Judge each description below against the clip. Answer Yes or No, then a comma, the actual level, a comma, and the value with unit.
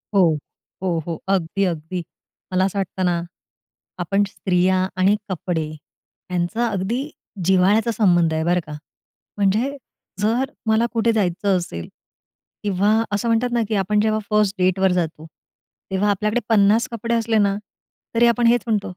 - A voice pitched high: Yes, high, 195 Hz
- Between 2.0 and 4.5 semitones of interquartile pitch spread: Yes, average, 3.4 semitones